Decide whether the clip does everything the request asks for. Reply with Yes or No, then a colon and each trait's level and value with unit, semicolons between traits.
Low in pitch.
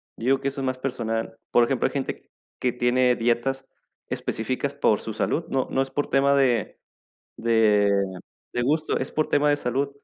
Yes: low, 130 Hz